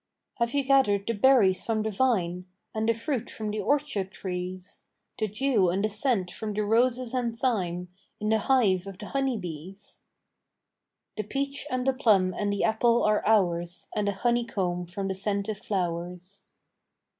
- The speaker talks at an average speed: Yes, average, 170 wpm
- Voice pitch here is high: Yes, high, 210 Hz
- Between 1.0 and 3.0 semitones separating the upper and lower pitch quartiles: No, average, 4.1 semitones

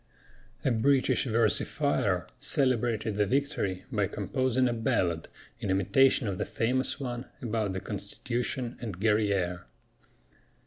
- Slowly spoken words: Yes, slow, 120 wpm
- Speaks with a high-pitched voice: No, low, 115 Hz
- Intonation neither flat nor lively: Yes, average, 4.1 semitones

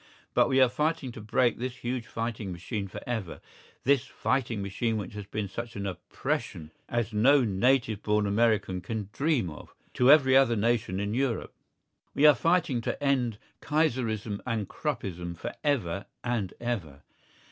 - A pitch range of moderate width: Yes, average, 4.2 semitones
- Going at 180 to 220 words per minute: No, average, 160 wpm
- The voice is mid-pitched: No, low, 115 Hz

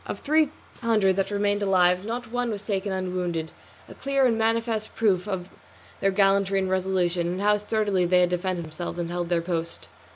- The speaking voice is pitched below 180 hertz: No, high, 190 Hz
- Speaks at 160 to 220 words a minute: Yes, average, 190 wpm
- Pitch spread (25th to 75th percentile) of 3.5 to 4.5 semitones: No, average, 3.0 semitones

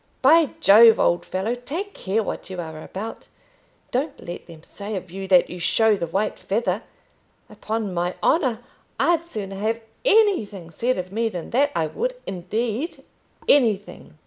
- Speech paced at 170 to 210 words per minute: No, average, 155 wpm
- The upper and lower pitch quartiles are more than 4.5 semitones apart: Yes, average, 5.0 semitones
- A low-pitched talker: No, high, 215 Hz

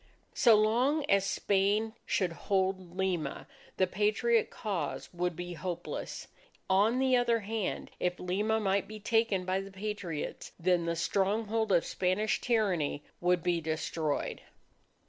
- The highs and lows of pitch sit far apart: No, average, 3.4 semitones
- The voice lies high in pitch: Yes, high, 195 Hz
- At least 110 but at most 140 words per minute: Yes, slow, 135 wpm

